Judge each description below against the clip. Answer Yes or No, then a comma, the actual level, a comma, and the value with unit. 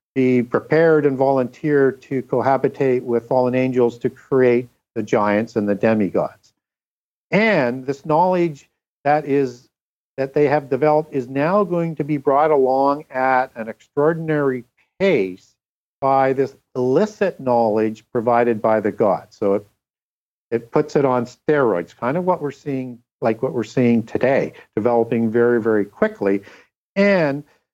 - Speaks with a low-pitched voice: Yes, low, 130 Hz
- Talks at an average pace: Yes, average, 145 wpm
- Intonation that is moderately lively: Yes, average, 3.7 semitones